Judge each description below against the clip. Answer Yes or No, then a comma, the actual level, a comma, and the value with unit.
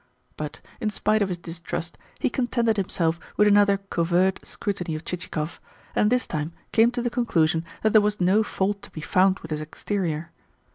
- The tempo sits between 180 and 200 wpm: Yes, average, 185 wpm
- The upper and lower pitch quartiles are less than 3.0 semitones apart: No, average, 4.0 semitones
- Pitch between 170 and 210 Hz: Yes, high, 190 Hz